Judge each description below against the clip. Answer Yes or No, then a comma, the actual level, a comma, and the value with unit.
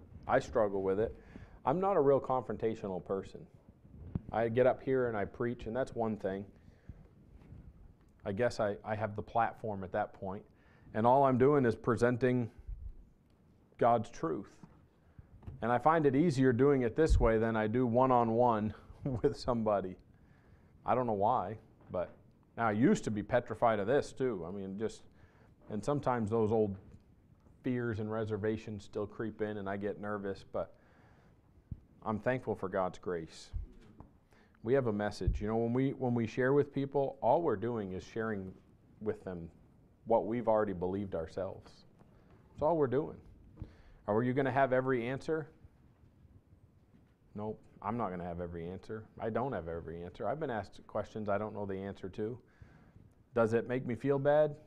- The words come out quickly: No, average, 170 wpm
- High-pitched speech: No, low, 110 Hz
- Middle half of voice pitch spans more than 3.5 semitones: Yes, average, 4.1 semitones